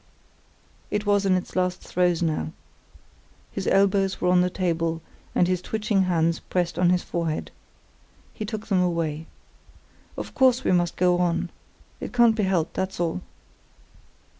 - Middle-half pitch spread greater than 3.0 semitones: No, narrow, 2.4 semitones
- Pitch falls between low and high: Yes, medium, 180 Hz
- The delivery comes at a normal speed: Yes, average, 155 wpm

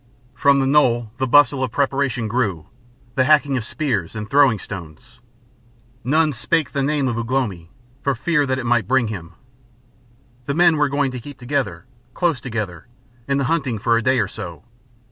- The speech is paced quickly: No, average, 185 wpm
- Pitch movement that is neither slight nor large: Yes, average, 4.0 semitones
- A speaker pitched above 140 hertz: No, low, 130 Hz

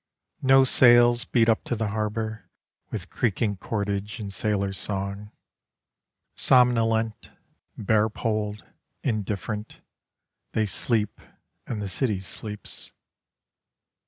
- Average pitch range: No, narrow, 2.0 semitones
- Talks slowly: Yes, slow, 100 wpm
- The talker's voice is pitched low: Yes, low, 110 Hz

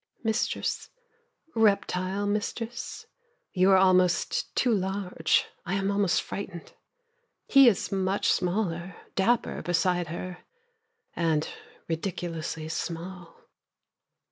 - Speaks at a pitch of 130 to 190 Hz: Yes, medium, 185 Hz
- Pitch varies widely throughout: No, average, 2.7 semitones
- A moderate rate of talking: No, slow, 90 wpm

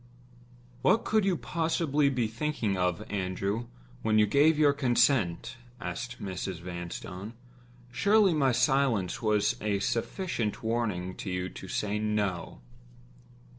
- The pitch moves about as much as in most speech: No, wide, 6.4 semitones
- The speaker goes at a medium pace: No, slow, 125 wpm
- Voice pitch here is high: No, low, 110 Hz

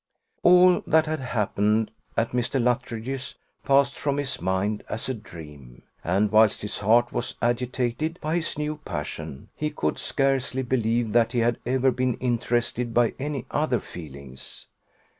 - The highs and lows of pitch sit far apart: No, average, 4.0 semitones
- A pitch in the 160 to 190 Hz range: No, low, 120 Hz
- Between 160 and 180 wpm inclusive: No, average, 150 wpm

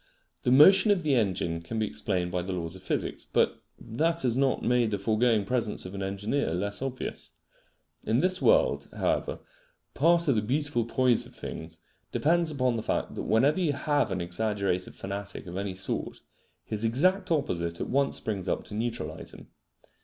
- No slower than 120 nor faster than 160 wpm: No, average, 185 wpm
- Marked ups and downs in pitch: Yes, wide, 6.5 semitones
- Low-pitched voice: Yes, low, 115 Hz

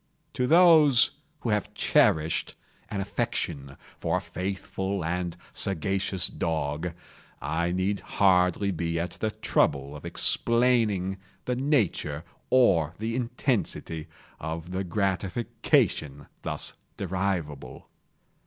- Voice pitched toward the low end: Yes, very low, 95 Hz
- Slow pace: Yes, slow, 105 wpm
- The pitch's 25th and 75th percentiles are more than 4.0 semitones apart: Yes, average, 4.6 semitones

